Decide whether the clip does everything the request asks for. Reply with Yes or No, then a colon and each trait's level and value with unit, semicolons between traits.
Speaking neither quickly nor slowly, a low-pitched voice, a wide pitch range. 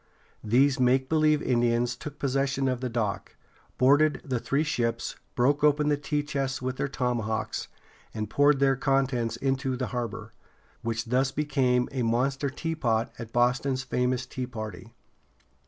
No: average, 150 wpm; low, 130 Hz; narrow, 2.5 semitones